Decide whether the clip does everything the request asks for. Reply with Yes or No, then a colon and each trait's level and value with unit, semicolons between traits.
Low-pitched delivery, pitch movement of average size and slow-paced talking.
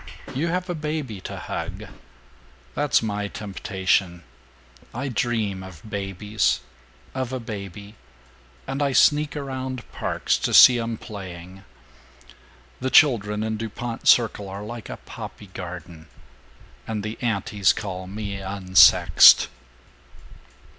Yes: low, 105 Hz; average, 4.4 semitones; slow, 120 wpm